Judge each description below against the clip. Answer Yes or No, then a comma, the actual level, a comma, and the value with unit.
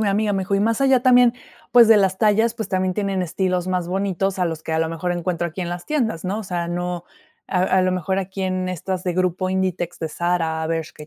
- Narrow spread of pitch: Yes, narrow, 2.2 semitones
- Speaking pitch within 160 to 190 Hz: Yes, medium, 185 Hz